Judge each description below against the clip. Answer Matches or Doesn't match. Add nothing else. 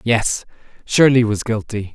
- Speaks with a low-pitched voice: Matches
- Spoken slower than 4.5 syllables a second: Matches